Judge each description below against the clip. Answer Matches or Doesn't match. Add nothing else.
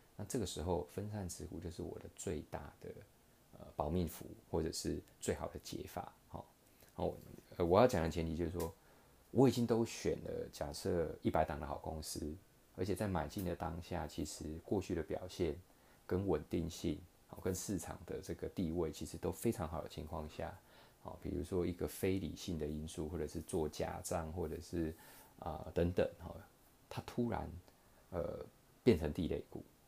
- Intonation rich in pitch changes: Doesn't match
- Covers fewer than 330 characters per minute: Matches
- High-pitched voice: Doesn't match